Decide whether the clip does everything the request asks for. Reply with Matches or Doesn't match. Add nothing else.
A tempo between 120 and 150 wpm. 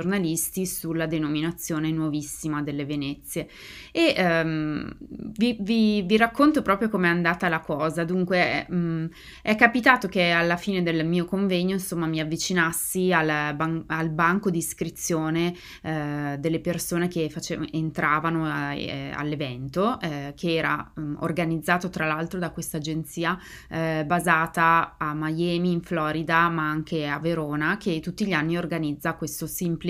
Matches